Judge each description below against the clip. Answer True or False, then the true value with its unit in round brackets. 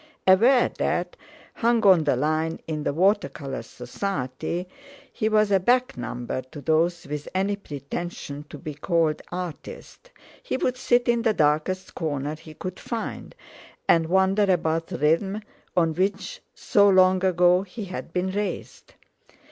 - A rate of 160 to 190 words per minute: False (150 wpm)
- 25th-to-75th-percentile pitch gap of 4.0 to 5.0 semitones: True (4.5 semitones)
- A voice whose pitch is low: False (180 Hz)